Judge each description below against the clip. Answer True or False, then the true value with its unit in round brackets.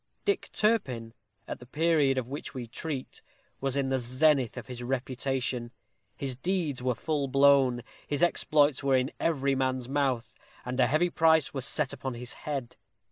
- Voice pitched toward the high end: False (135 Hz)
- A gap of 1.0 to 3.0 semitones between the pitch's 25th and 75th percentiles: True (2.6 semitones)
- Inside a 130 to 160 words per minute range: False (170 wpm)